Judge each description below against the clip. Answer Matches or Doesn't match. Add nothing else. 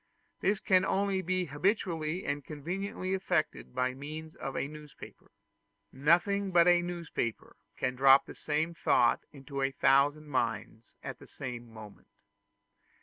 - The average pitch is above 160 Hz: Doesn't match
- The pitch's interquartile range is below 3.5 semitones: Doesn't match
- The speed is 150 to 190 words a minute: Doesn't match